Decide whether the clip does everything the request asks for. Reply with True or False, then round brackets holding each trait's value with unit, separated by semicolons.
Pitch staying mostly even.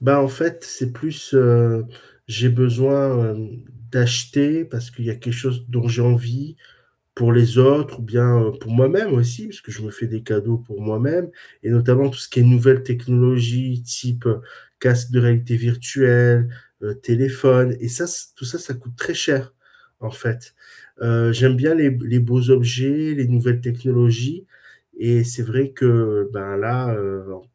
True (1.8 semitones)